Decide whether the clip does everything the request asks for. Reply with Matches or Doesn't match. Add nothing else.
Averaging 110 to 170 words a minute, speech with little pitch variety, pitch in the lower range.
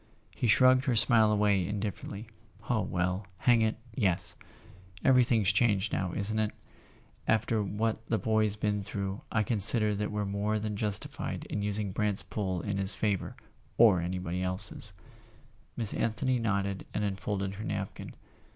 Matches